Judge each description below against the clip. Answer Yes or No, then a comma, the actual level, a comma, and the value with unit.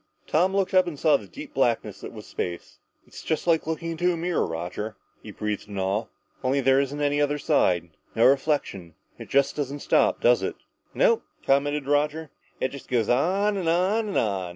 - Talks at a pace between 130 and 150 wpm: No, average, 195 wpm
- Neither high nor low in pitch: Yes, medium, 145 Hz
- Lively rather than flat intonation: Yes, wide, 6.7 semitones